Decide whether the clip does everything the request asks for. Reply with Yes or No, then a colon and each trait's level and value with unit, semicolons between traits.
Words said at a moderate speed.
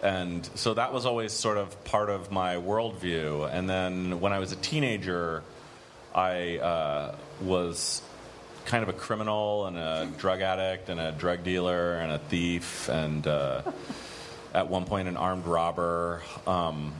Yes: average, 160 wpm